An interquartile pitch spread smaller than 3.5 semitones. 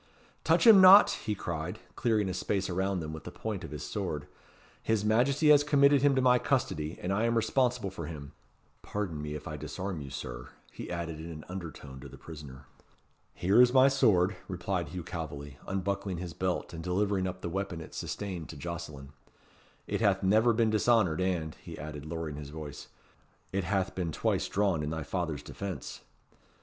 No: average, 5.1 semitones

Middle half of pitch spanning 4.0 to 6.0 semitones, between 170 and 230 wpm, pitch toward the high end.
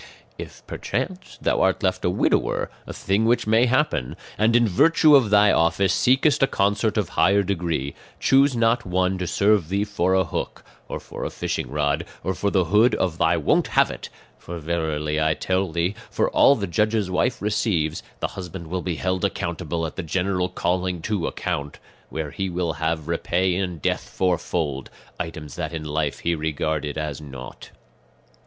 No: average, 4.4 semitones; average, 180 wpm; very low, 90 Hz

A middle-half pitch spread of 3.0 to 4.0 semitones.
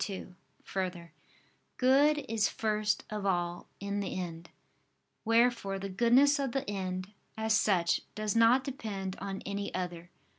Yes: average, 3.6 semitones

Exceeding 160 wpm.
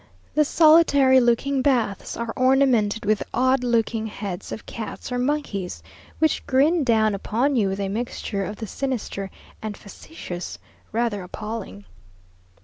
No: average, 140 wpm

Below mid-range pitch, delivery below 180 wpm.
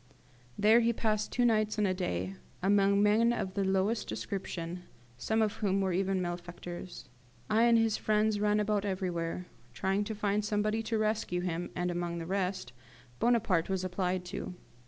No: high, 195 Hz; average, 170 wpm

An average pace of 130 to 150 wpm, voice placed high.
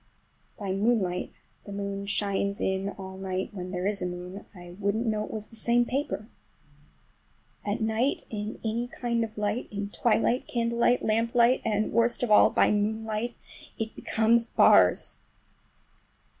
Yes: average, 145 wpm; high, 215 Hz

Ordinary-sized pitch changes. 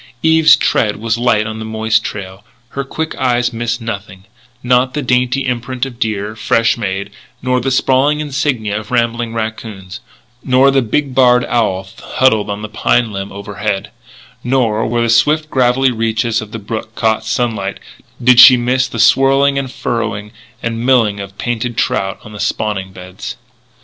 Yes: average, 3.1 semitones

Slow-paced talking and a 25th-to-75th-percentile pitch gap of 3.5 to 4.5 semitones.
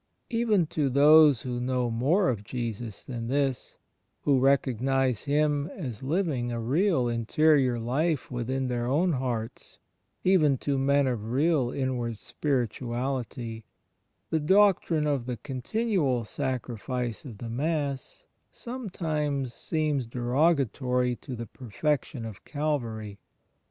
Yes: slow, 125 wpm; average, 3.8 semitones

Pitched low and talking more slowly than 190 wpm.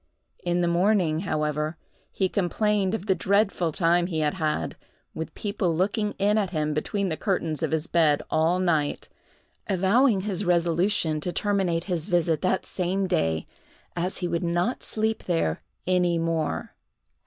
No: medium, 175 Hz; average, 155 wpm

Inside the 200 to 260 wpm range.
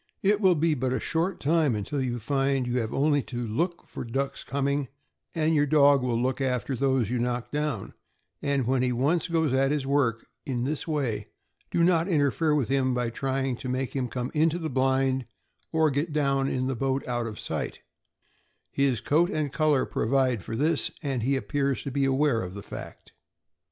Yes: fast, 205 wpm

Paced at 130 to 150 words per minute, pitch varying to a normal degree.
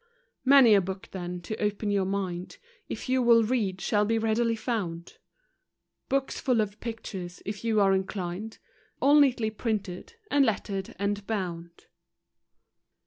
Yes: average, 145 wpm; average, 3.3 semitones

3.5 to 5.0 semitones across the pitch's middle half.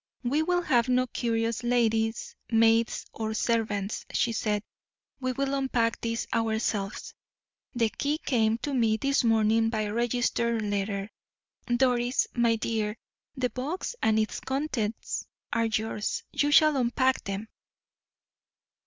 No: narrow, 2.6 semitones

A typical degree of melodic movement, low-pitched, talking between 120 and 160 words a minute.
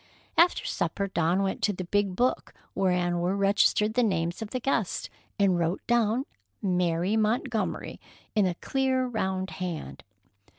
No: average, 3.7 semitones; high, 195 Hz; average, 145 wpm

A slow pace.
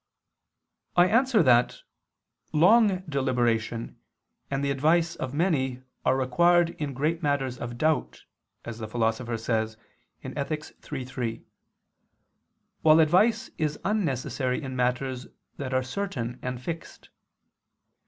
Yes: slow, 115 wpm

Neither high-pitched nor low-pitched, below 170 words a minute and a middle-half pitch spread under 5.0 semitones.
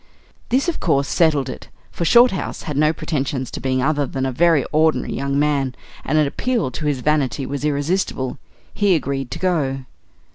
No: medium, 145 Hz; average, 180 wpm; average, 3.1 semitones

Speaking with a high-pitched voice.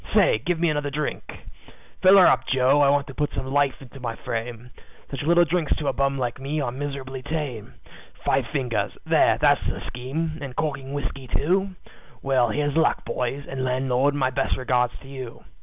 No: low, 135 Hz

